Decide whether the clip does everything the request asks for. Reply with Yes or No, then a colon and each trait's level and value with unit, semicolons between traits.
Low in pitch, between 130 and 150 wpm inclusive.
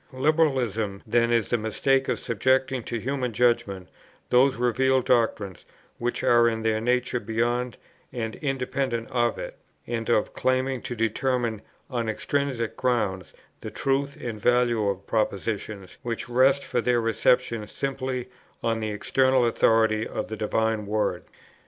Yes: low, 120 Hz; average, 140 wpm